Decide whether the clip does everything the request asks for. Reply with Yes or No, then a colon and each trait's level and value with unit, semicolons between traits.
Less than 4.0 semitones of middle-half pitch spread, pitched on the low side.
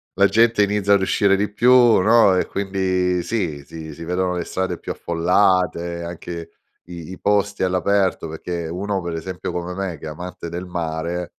Yes: narrow, 2.5 semitones; very low, 90 Hz